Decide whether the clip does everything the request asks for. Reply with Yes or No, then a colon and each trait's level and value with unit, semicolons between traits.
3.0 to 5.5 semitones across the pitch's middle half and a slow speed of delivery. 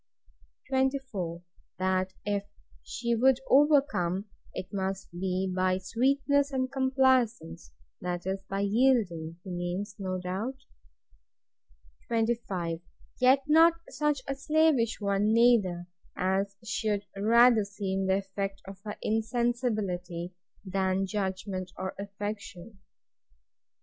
Yes: average, 4.5 semitones; slow, 105 wpm